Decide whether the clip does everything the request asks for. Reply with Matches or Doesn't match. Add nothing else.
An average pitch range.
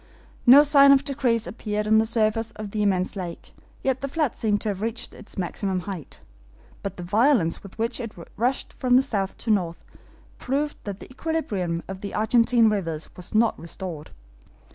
Matches